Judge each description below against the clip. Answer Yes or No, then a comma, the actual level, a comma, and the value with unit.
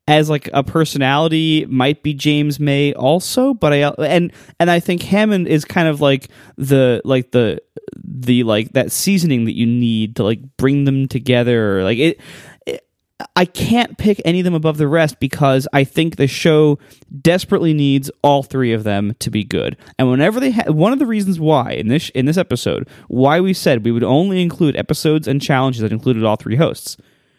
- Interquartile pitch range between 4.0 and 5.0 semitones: Yes, average, 4.3 semitones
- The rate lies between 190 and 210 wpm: Yes, average, 200 wpm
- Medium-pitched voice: Yes, medium, 145 Hz